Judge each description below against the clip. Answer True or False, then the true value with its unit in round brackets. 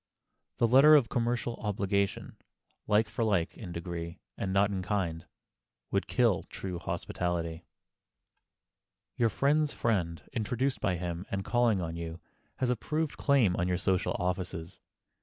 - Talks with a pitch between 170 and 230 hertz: False (100 Hz)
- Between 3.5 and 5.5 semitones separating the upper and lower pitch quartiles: True (5.2 semitones)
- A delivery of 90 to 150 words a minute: True (140 wpm)